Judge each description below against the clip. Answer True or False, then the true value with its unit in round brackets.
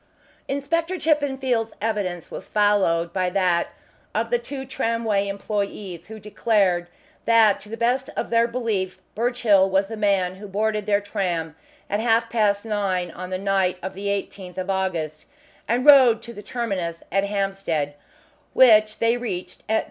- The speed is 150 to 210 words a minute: True (160 wpm)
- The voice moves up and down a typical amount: True (3.4 semitones)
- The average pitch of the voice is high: True (205 Hz)